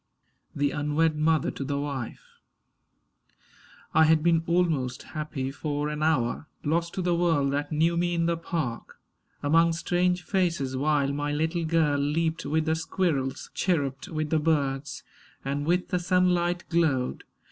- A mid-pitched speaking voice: Yes, medium, 155 Hz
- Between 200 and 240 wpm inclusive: No, average, 150 wpm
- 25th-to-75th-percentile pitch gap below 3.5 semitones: Yes, average, 2.8 semitones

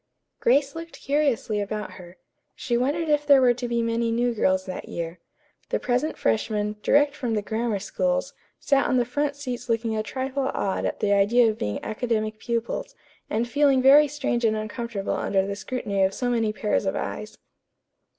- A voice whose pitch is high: Yes, high, 235 Hz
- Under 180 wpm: No, average, 185 wpm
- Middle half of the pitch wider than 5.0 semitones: No, average, 4.2 semitones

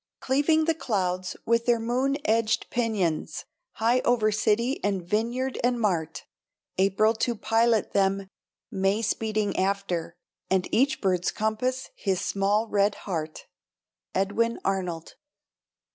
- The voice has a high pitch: Yes, high, 215 Hz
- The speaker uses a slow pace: Yes, slow, 120 wpm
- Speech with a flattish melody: No, average, 3.4 semitones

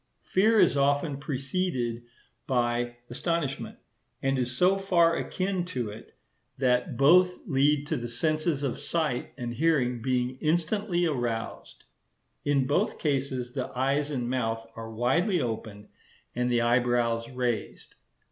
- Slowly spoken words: Yes, slow, 130 wpm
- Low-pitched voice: Yes, low, 130 Hz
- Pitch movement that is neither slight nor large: Yes, average, 4.7 semitones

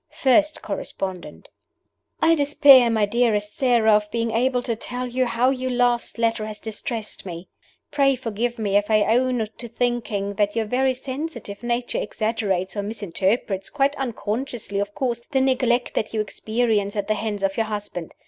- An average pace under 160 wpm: No, average, 165 wpm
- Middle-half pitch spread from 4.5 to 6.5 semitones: No, average, 3.3 semitones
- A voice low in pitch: No, high, 230 Hz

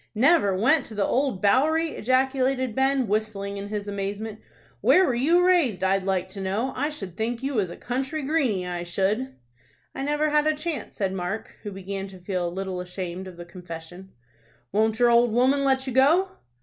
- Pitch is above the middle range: Yes, high, 220 Hz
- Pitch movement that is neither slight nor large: No, wide, 5.8 semitones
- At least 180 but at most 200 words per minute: Yes, average, 195 wpm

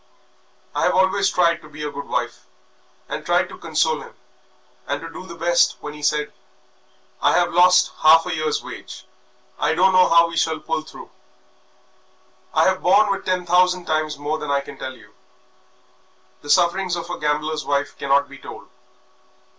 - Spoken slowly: No, average, 180 wpm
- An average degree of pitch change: Yes, average, 3.3 semitones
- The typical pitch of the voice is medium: Yes, medium, 165 Hz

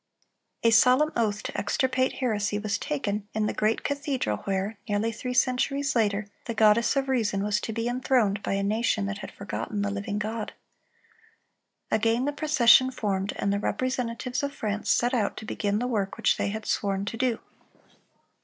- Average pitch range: Yes, average, 3.7 semitones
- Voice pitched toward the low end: No, high, 220 Hz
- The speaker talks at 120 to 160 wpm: No, average, 180 wpm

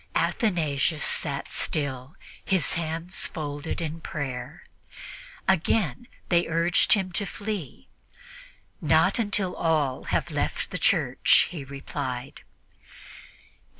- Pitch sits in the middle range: Yes, medium, 160 Hz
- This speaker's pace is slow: Yes, slow, 100 wpm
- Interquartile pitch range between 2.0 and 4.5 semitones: Yes, average, 4.2 semitones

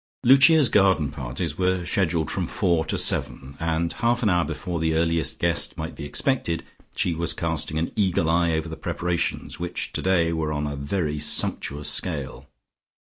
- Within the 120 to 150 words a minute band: No, average, 170 wpm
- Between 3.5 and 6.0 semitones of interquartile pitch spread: No, narrow, 2.5 semitones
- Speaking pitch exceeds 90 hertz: No, very low, 85 Hz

